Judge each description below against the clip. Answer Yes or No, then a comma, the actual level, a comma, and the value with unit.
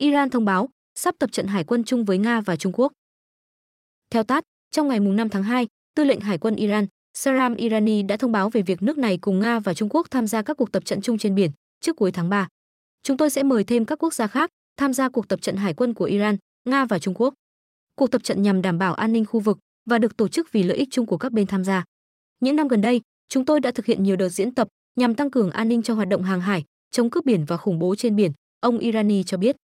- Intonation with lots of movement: No, average, 4.4 semitones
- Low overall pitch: No, high, 225 Hz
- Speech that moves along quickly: Yes, fast, 270 wpm